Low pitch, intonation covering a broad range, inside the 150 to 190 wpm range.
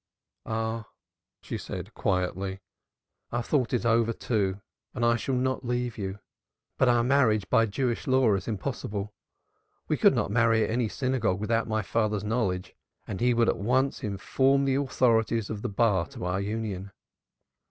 No: low, 115 Hz; average, 3.3 semitones; average, 170 wpm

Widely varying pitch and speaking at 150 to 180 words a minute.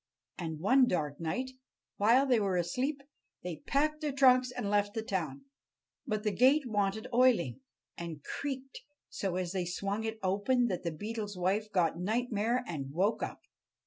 Yes: wide, 5.8 semitones; average, 165 wpm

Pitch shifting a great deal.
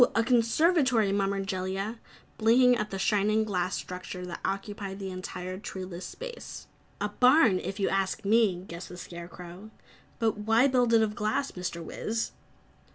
No: average, 3.5 semitones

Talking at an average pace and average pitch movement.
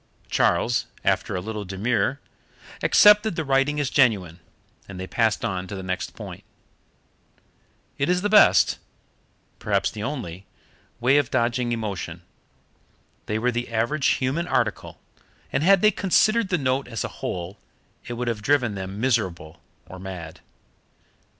No: average, 145 wpm; wide, 6.5 semitones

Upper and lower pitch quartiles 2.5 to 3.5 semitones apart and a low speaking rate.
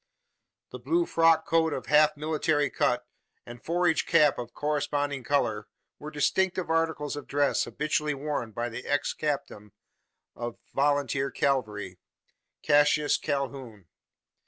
Yes: average, 2.8 semitones; slow, 125 wpm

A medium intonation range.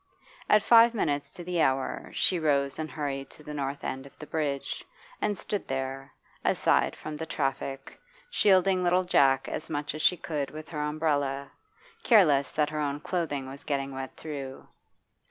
Yes: average, 3.1 semitones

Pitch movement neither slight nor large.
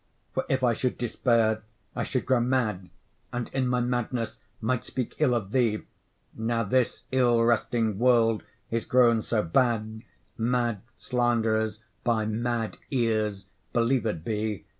No: narrow, 2.1 semitones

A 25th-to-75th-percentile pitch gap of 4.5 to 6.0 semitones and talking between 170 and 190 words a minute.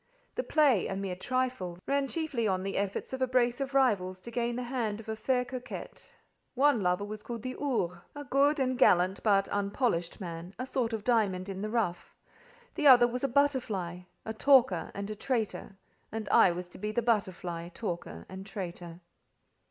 Yes: wide, 5.4 semitones; average, 185 wpm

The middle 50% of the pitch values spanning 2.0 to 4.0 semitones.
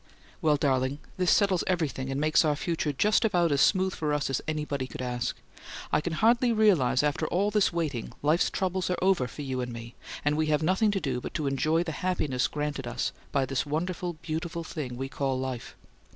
No: average, 4.8 semitones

